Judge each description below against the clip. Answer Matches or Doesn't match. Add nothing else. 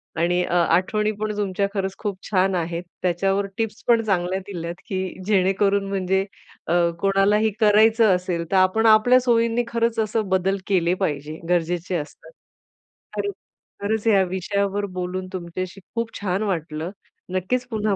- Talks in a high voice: Matches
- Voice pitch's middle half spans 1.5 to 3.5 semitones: Matches